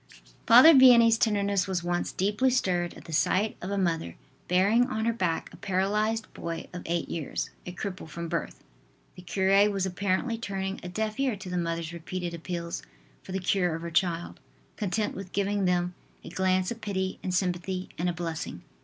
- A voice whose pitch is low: No, medium, 185 Hz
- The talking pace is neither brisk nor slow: Yes, average, 190 wpm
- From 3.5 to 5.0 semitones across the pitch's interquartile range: No, average, 2.8 semitones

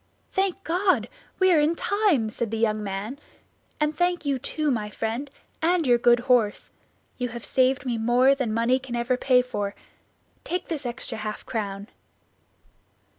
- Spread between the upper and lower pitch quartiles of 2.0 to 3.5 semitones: No, average, 5.1 semitones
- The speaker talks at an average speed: Yes, average, 165 wpm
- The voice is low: No, very high, 250 Hz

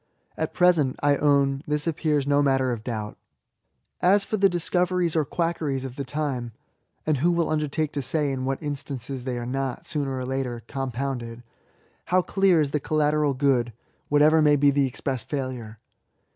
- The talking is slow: No, average, 185 wpm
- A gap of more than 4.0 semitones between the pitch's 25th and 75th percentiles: No, average, 3.0 semitones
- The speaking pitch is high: No, medium, 140 Hz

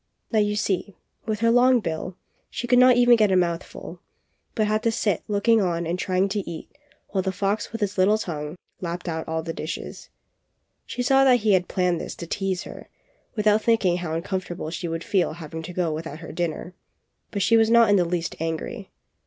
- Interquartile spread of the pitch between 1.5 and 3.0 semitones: No, average, 4.2 semitones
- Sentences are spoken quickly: Yes, fast, 210 wpm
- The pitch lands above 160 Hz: Yes, high, 190 Hz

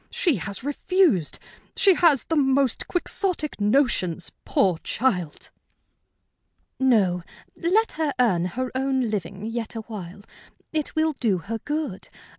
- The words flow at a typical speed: No, slow, 120 wpm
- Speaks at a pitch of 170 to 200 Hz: No, high, 245 Hz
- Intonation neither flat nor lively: No, wide, 7.3 semitones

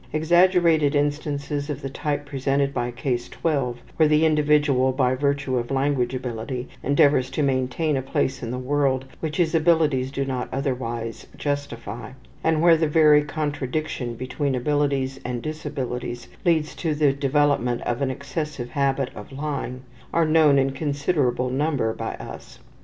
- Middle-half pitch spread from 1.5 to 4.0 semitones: Yes, average, 2.8 semitones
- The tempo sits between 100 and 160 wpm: Yes, average, 155 wpm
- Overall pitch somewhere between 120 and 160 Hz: Yes, medium, 140 Hz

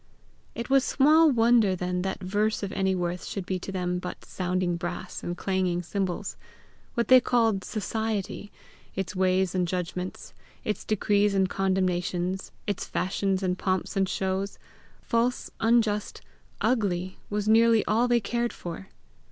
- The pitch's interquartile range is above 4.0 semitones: No, average, 3.1 semitones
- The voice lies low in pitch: No, high, 195 Hz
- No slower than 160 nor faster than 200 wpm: No, average, 145 wpm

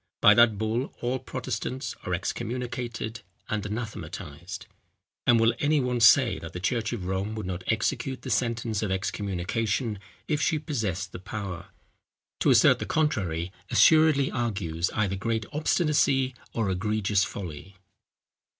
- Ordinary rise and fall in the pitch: Yes, average, 4.6 semitones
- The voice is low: Yes, low, 110 Hz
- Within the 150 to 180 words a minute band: No, average, 140 wpm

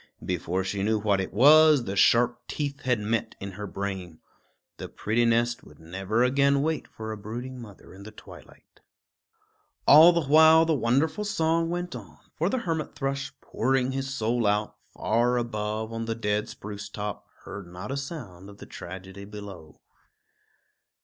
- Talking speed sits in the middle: Yes, average, 170 wpm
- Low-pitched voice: Yes, low, 115 Hz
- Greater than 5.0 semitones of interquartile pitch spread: Yes, wide, 5.4 semitones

